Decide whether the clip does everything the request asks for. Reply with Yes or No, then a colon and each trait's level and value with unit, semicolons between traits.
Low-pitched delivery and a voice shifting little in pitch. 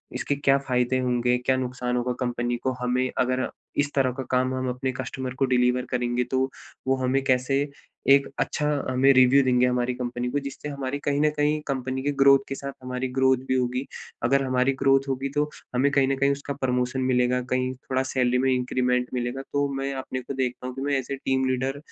Yes: low, 130 Hz; narrow, 1.4 semitones